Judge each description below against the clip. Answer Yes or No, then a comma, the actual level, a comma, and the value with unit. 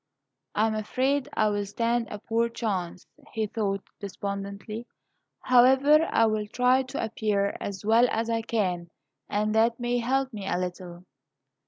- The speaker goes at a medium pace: Yes, average, 155 wpm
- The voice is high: Yes, high, 220 Hz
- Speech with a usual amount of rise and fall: Yes, average, 3.1 semitones